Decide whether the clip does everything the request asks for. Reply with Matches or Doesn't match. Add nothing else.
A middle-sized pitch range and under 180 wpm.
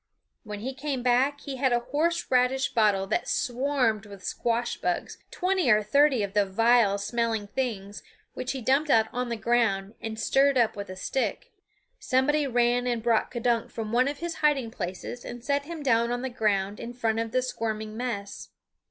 Doesn't match